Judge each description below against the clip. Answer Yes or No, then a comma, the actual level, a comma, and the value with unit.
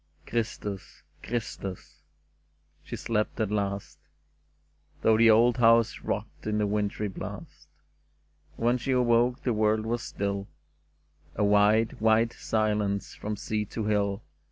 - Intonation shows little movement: Yes, narrow, 2.1 semitones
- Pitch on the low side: Yes, low, 110 Hz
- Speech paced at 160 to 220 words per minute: No, slow, 135 wpm